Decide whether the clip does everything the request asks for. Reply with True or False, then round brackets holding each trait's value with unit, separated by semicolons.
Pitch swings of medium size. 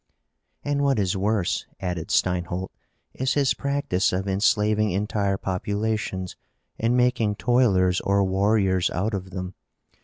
True (3.1 semitones)